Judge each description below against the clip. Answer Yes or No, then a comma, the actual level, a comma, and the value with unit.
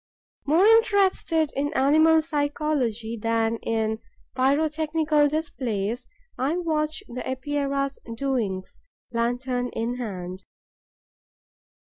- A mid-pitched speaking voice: No, very high, 275 Hz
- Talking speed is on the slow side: Yes, slow, 85 wpm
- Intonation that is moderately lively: Yes, average, 4.9 semitones